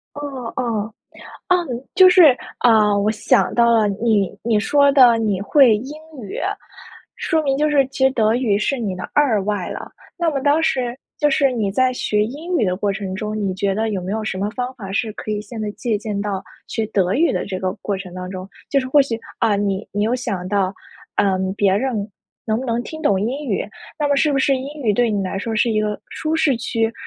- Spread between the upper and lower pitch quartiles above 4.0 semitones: Yes, average, 4.6 semitones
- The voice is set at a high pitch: Yes, high, 220 Hz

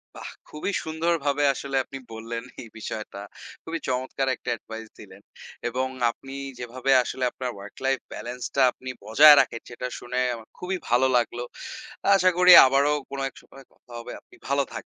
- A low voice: Yes, low, 130 Hz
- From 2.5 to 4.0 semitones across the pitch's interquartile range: Yes, average, 3.1 semitones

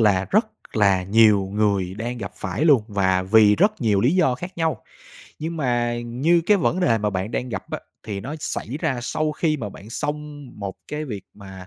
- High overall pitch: No, low, 115 Hz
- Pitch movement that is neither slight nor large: No, wide, 7.0 semitones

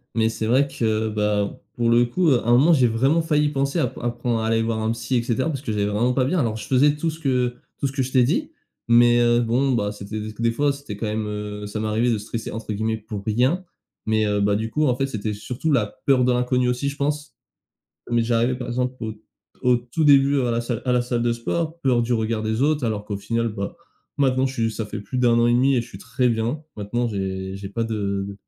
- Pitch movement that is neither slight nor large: Yes, average, 3.2 semitones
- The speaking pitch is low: Yes, low, 120 Hz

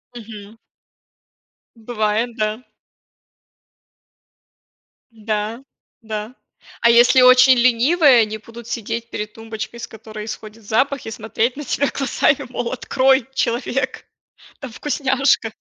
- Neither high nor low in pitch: No, high, 230 Hz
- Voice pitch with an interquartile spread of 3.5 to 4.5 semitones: No, average, 2.7 semitones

